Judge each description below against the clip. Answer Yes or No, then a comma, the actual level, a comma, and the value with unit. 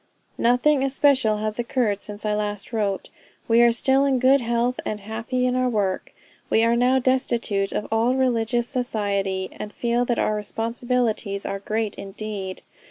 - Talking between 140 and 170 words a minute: Yes, average, 165 wpm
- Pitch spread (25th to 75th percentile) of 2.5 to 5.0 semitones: Yes, average, 3.1 semitones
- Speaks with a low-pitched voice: No, high, 230 Hz